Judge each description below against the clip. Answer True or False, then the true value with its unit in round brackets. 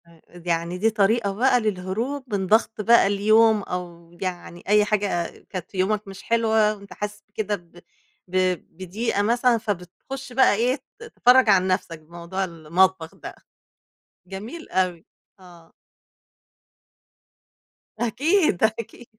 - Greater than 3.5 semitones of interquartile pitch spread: True (3.9 semitones)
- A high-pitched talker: True (205 Hz)